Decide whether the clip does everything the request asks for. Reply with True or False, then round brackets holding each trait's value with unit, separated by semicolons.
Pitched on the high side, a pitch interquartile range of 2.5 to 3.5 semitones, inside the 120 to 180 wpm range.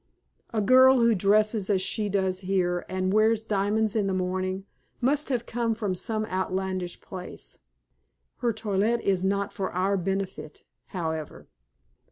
True (195 Hz; 2.8 semitones; 145 wpm)